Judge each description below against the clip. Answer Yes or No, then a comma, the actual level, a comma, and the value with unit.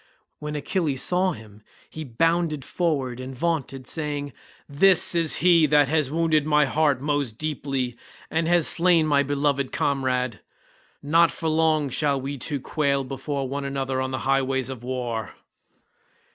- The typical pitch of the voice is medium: Yes, medium, 145 Hz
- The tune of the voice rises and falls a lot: No, average, 3.0 semitones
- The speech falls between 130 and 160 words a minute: Yes, average, 150 wpm